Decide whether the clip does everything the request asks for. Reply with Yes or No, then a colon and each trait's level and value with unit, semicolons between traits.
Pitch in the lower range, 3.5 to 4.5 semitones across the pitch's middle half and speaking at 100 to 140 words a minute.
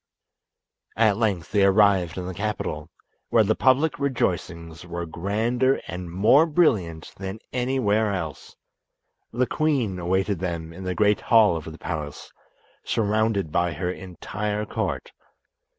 Yes: low, 100 Hz; average, 4.2 semitones; slow, 135 wpm